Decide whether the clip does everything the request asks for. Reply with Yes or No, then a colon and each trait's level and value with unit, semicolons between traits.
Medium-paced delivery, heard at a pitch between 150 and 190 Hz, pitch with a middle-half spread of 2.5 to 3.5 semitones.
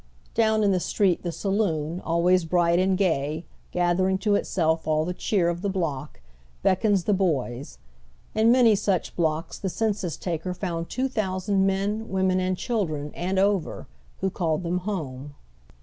Yes: average, 165 wpm; medium, 185 Hz; average, 3.1 semitones